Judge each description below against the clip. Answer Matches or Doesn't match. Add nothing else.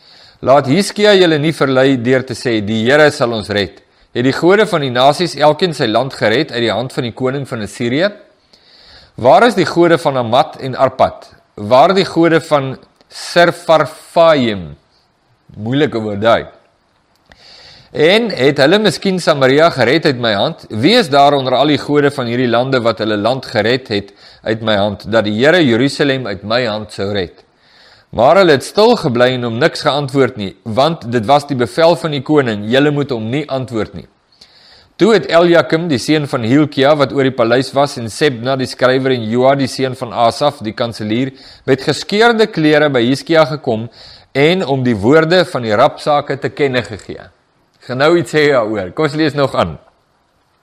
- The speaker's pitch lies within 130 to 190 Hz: Matches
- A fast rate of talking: Doesn't match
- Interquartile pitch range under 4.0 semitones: Doesn't match